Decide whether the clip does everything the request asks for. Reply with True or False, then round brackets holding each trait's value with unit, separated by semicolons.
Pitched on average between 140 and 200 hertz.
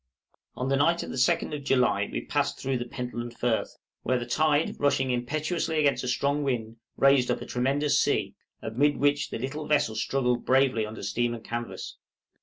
False (130 Hz)